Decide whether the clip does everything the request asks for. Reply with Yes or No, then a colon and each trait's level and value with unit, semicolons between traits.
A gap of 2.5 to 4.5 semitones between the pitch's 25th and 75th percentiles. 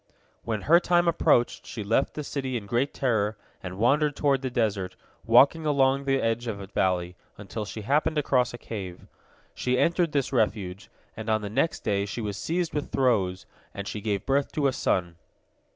No: wide, 5.4 semitones